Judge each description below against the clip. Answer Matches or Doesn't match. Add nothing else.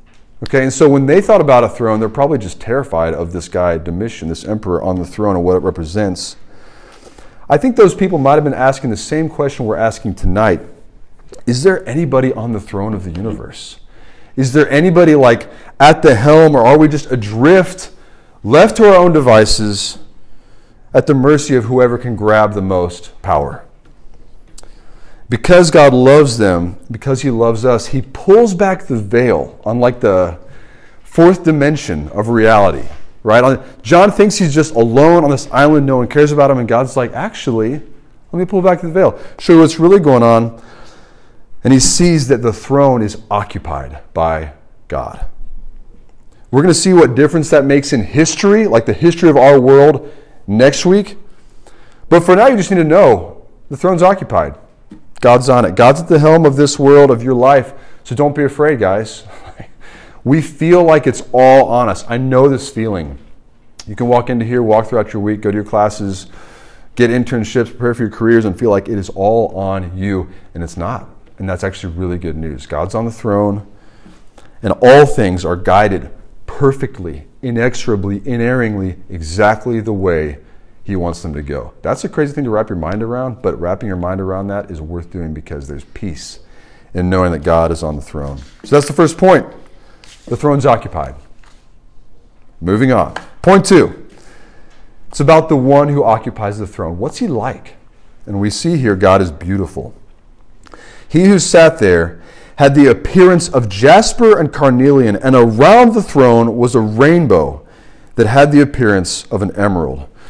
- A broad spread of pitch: Matches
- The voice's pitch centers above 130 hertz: Doesn't match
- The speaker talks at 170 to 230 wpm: Matches